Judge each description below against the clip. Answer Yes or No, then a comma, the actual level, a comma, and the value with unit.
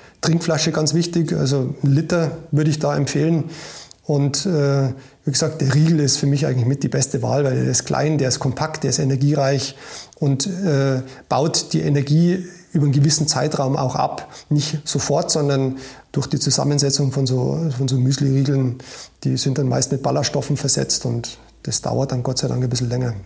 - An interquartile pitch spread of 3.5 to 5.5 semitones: No, narrow, 2.5 semitones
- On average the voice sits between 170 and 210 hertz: No, medium, 140 Hz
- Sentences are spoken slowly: No, fast, 190 wpm